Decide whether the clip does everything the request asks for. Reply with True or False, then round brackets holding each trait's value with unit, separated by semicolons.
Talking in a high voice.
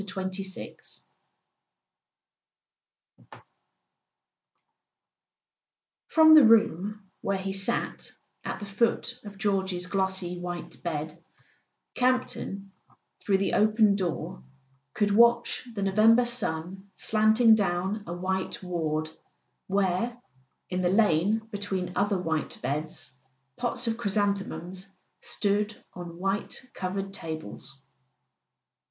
True (195 Hz)